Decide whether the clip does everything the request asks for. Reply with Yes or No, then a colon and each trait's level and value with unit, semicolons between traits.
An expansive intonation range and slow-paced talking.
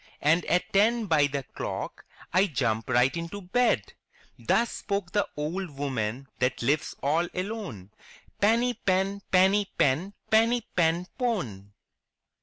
Yes: wide, 6.5 semitones; slow, 130 wpm